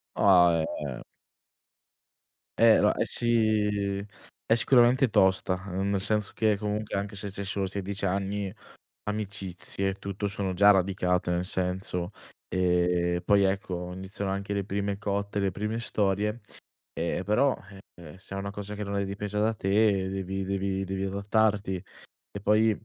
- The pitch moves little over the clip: Yes, narrow, 1.7 semitones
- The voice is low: Yes, low, 100 Hz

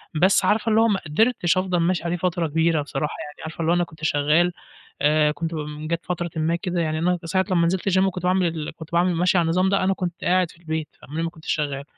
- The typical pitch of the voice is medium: Yes, medium, 170 Hz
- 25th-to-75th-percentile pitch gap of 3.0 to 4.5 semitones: No, narrow, 2.5 semitones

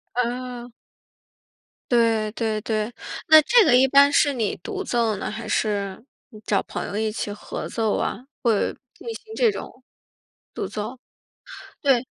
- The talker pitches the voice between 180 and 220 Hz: No, high, 235 Hz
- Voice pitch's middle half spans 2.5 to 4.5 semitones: Yes, average, 3.8 semitones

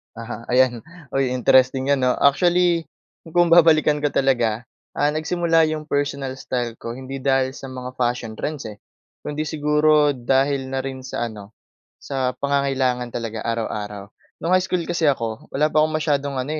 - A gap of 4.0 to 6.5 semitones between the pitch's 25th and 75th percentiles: No, average, 3.5 semitones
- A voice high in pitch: No, low, 135 Hz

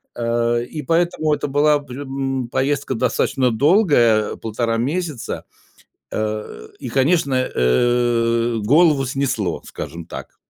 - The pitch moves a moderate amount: Yes, average, 3.7 semitones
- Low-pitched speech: Yes, low, 130 Hz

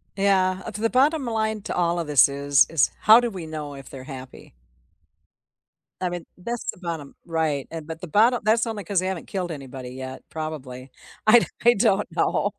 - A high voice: No, medium, 175 Hz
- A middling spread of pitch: No, wide, 6.9 semitones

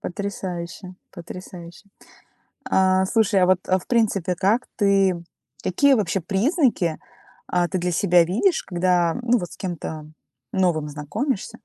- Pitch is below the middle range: No, medium, 185 Hz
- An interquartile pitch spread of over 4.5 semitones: No, average, 2.8 semitones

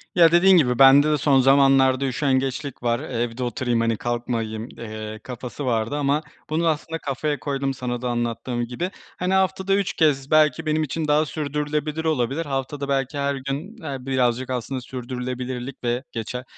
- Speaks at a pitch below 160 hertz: Yes, low, 135 Hz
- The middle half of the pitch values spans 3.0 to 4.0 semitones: Yes, average, 3.5 semitones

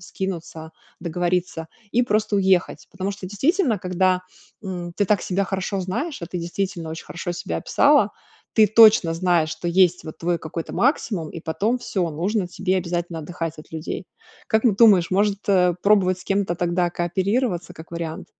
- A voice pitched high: No, medium, 180 Hz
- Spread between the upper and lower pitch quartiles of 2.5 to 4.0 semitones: Yes, average, 2.9 semitones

